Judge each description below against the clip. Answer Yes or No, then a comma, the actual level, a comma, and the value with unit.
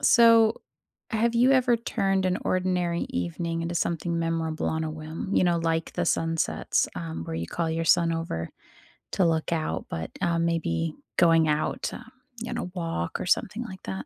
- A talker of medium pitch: Yes, medium, 165 Hz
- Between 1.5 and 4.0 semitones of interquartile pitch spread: Yes, average, 2.7 semitones